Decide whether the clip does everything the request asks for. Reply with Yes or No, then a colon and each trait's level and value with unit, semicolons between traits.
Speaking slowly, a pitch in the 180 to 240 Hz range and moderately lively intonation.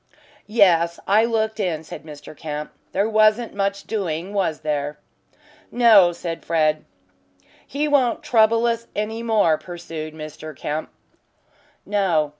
No: slow, 125 wpm; high, 190 Hz; wide, 5.8 semitones